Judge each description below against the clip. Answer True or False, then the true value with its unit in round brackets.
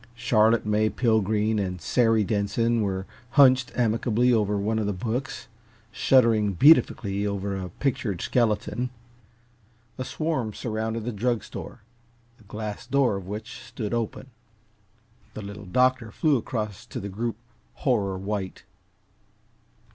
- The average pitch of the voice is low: True (110 Hz)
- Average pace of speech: False (130 wpm)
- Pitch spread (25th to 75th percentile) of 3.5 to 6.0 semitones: False (3.1 semitones)